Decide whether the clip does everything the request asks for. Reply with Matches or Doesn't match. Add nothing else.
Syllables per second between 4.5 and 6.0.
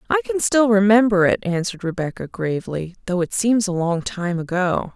Matches